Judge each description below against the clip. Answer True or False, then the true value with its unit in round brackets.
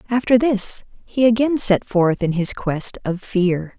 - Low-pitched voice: False (205 Hz)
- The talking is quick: False (175 wpm)